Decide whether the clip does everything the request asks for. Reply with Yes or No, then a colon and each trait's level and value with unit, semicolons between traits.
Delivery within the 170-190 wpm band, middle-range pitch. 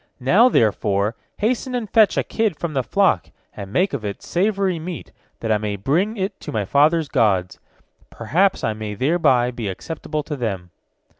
Yes: average, 175 wpm; medium, 145 Hz